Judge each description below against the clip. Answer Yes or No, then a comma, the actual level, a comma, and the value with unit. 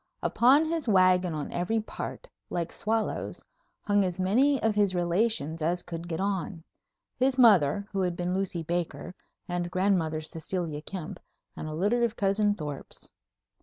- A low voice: No, medium, 185 Hz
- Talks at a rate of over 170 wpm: No, average, 155 wpm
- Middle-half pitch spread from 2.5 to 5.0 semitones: Yes, average, 3.7 semitones